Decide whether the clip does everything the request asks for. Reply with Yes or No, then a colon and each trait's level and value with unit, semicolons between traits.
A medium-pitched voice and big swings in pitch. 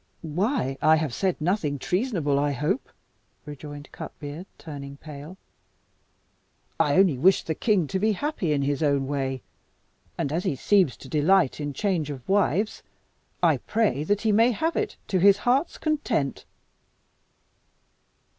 Yes: medium, 160 Hz; wide, 6.1 semitones